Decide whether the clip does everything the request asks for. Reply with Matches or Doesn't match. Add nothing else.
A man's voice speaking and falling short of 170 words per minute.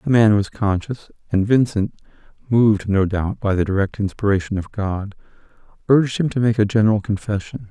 Matches